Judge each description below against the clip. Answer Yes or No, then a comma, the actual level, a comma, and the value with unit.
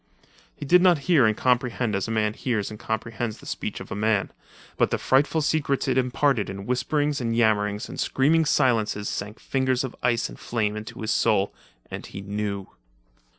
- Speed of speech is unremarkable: Yes, average, 180 wpm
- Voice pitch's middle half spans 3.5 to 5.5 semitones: Yes, average, 4.0 semitones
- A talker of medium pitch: No, low, 115 Hz